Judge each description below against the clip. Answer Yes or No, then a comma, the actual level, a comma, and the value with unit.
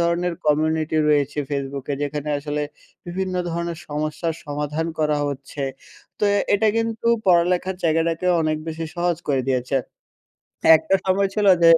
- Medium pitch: Yes, medium, 160 Hz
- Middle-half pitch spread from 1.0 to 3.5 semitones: Yes, average, 2.8 semitones